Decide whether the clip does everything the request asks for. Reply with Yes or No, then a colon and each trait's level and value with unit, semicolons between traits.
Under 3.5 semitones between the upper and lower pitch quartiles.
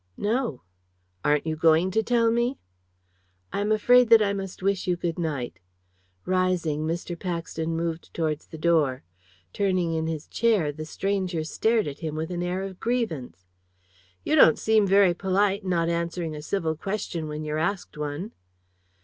No: average, 4.0 semitones